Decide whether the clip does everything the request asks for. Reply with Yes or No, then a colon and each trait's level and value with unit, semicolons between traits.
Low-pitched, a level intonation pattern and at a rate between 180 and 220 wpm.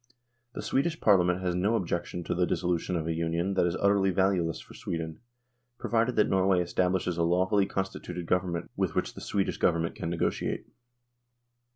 Yes: very low, 90 Hz; narrow, 2.1 semitones; average, 185 wpm